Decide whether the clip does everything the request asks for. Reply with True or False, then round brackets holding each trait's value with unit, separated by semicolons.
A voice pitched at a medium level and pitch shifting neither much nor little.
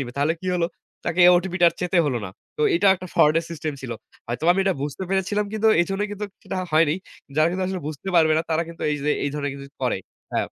True (165 Hz; 4.0 semitones)